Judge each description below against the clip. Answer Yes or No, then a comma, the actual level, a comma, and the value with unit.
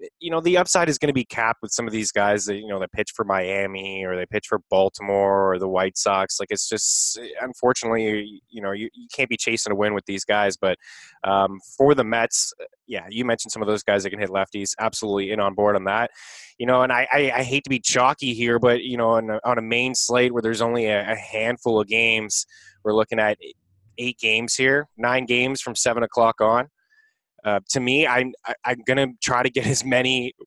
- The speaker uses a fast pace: Yes, fast, 235 wpm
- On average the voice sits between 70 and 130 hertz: Yes, low, 115 Hz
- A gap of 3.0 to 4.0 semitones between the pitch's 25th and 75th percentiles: Yes, average, 3.6 semitones